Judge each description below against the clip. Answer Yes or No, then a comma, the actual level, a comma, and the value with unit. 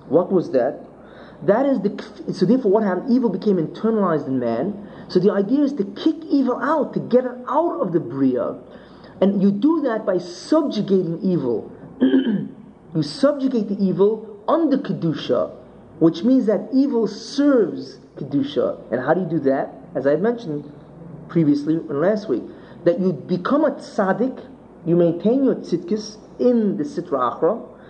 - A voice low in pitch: No, high, 205 Hz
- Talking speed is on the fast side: No, average, 165 wpm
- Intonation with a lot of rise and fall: Yes, wide, 6.2 semitones